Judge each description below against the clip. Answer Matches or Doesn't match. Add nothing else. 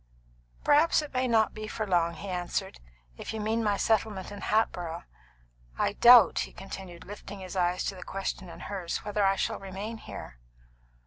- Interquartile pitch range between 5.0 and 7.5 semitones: Doesn't match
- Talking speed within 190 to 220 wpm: Doesn't match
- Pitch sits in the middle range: Doesn't match